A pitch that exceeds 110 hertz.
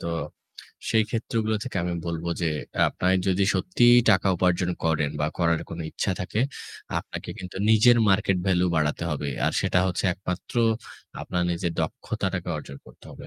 No: very low, 90 Hz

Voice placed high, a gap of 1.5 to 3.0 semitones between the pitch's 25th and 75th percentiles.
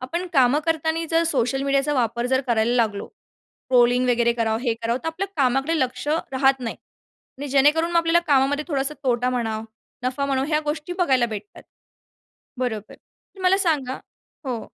No: very high, 265 Hz; average, 3.9 semitones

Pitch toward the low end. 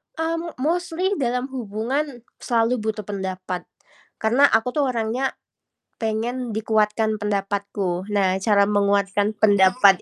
No: high, 220 Hz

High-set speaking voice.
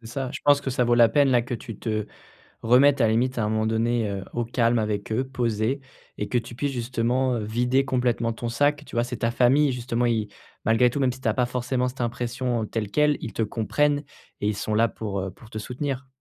No: low, 120 Hz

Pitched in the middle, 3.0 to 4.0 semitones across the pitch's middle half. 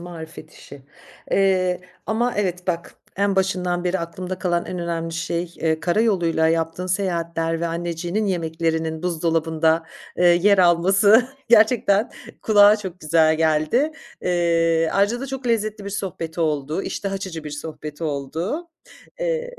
Yes: medium, 175 Hz; average, 3.4 semitones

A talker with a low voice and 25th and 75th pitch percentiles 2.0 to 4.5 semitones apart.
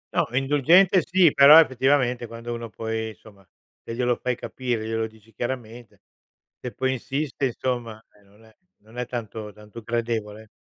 Yes: low, 120 Hz; average, 2.8 semitones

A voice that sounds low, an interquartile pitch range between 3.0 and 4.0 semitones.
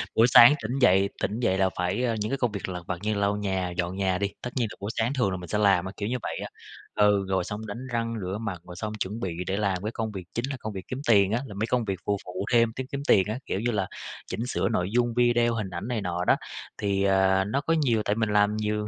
Yes: low, 105 Hz; average, 3.4 semitones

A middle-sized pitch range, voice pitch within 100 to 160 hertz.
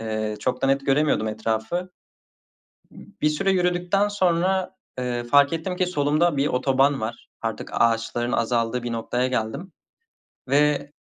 No: wide, 6.7 semitones; medium, 140 Hz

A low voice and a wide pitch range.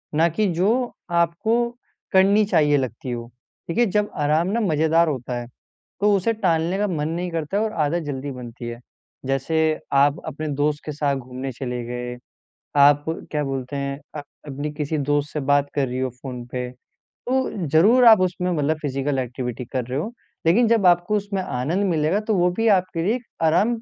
No: medium, 155 Hz; wide, 5.7 semitones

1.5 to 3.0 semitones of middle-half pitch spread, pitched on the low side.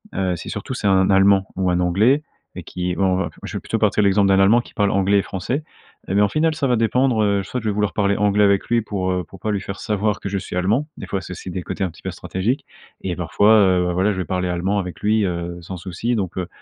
Yes: narrow, 2.4 semitones; low, 100 Hz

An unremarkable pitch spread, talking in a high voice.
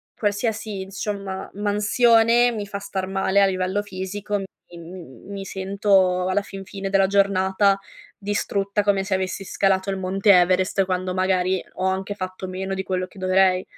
No: narrow, 1.3 semitones; high, 195 Hz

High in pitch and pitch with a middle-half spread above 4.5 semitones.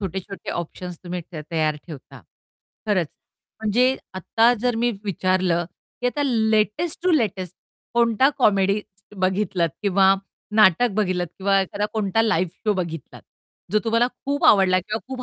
No: high, 200 Hz; average, 3.6 semitones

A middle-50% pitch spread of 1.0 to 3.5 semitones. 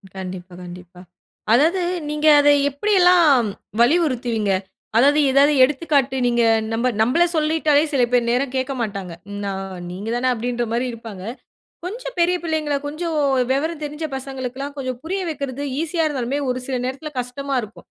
No: average, 4.3 semitones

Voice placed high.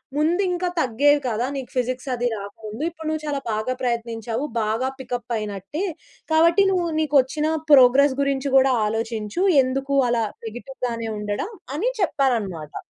Yes: very high, 255 Hz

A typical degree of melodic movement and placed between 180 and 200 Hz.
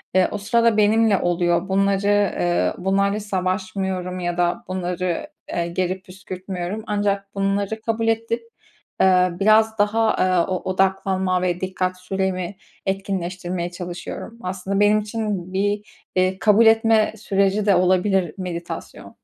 No: narrow, 2.1 semitones; high, 190 Hz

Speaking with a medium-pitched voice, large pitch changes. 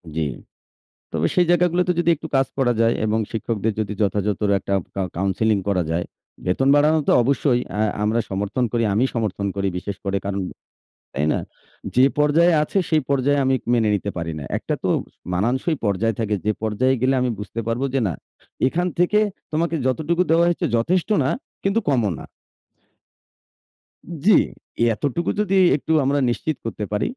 No: low, 120 Hz; wide, 6.8 semitones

